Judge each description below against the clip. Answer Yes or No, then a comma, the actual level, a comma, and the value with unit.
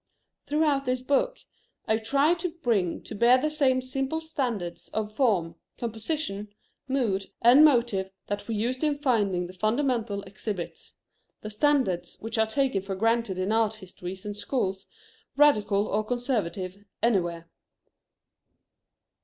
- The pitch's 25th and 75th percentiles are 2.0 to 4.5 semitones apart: No, average, 5.2 semitones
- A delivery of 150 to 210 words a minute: No, slow, 135 wpm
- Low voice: No, high, 225 Hz